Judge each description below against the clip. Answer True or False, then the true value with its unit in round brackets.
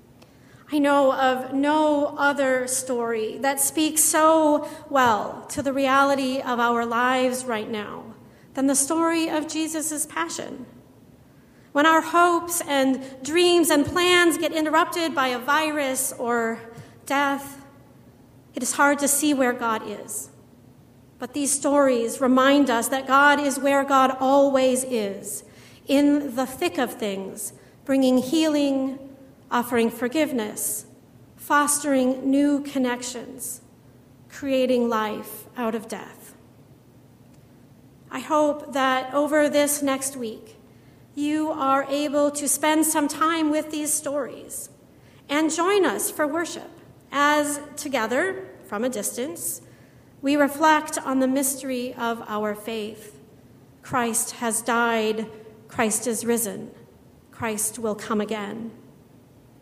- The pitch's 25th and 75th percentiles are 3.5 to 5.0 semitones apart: True (3.9 semitones)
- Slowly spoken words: True (120 wpm)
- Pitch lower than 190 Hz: False (270 Hz)